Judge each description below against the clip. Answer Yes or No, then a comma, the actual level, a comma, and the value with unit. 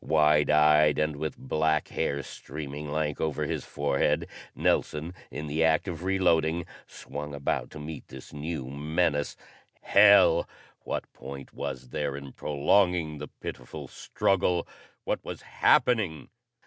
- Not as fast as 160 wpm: Yes, slow, 135 wpm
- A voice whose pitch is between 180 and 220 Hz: No, very low, 75 Hz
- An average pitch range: No, narrow, 2.0 semitones